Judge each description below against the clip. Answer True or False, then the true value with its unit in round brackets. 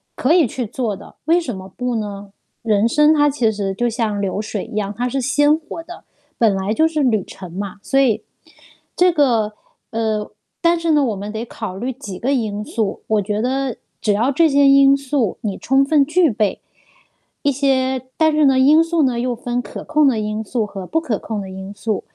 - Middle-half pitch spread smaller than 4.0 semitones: False (5.0 semitones)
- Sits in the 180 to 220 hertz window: False (240 Hz)